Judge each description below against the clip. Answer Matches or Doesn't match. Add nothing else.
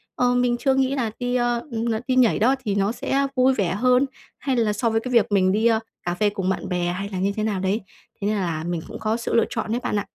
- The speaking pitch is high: Matches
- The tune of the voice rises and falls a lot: Doesn't match